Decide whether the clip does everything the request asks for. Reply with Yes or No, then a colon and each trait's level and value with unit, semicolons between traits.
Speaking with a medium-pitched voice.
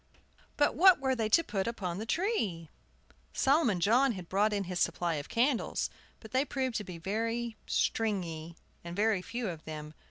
No: high, 215 Hz